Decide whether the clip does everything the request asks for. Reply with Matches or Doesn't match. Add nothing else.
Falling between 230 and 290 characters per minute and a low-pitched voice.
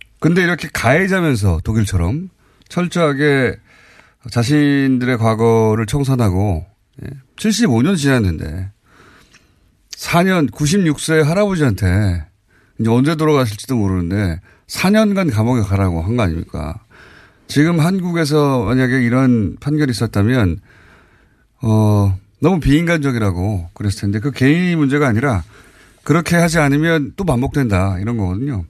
Matches